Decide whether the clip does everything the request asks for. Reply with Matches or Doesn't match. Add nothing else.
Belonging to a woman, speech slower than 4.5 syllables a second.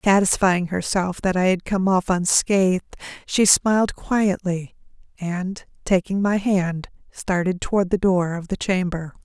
Matches